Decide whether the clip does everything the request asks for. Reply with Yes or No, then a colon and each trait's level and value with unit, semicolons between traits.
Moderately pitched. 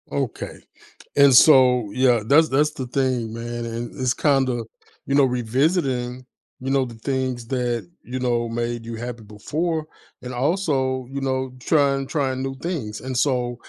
No: low, 130 Hz